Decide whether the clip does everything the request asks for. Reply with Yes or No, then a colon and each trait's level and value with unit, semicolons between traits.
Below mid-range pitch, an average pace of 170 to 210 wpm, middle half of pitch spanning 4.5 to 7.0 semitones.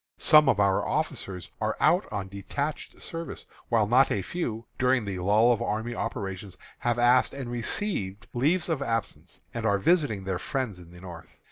Yes: low, 115 Hz; average, 175 wpm; average, 5.1 semitones